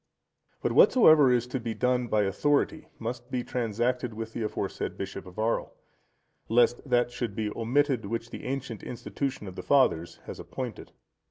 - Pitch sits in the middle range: No, low, 120 Hz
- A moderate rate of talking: Yes, average, 165 wpm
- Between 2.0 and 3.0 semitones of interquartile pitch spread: Yes, narrow, 2.4 semitones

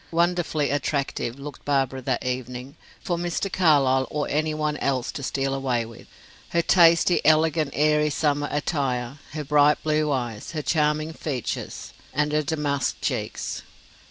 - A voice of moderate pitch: Yes, medium, 150 Hz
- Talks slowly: No, average, 145 wpm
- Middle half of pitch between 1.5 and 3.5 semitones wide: Yes, narrow, 2.4 semitones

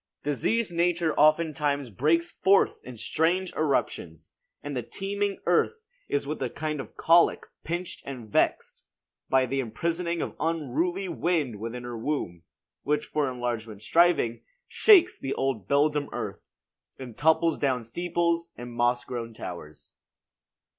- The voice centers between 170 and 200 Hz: No, medium, 145 Hz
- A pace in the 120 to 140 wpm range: Yes, slow, 135 wpm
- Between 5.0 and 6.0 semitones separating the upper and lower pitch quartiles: Yes, wide, 5.6 semitones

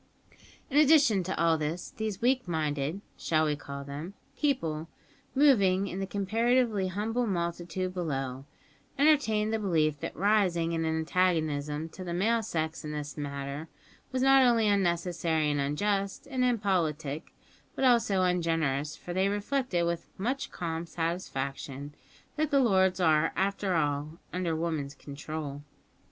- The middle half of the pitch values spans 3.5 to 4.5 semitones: No, average, 5.2 semitones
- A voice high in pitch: No, medium, 175 Hz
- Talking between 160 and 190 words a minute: No, average, 140 wpm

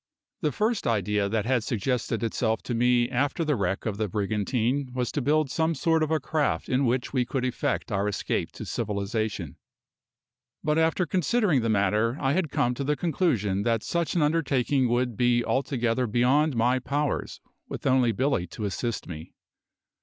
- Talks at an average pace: Yes, average, 175 wpm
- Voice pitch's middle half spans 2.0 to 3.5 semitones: No, average, 4.7 semitones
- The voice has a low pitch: Yes, low, 125 Hz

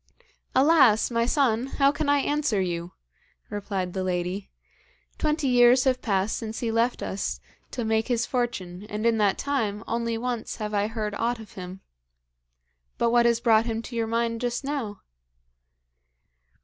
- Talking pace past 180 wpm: No, average, 160 wpm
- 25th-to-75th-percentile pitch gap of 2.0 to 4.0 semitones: Yes, average, 2.9 semitones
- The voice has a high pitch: Yes, high, 230 Hz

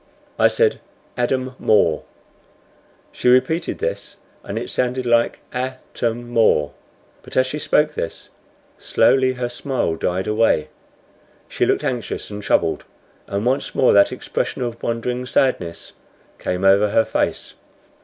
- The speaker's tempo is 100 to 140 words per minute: Yes, slow, 135 wpm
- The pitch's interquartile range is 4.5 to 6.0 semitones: No, average, 3.9 semitones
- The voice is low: Yes, low, 120 Hz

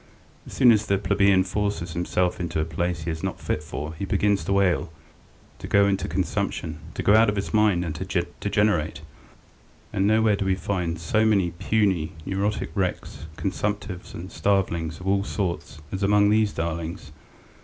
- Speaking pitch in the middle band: No, very low, 95 Hz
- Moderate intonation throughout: Yes, average, 3.3 semitones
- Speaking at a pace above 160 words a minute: Yes, average, 175 wpm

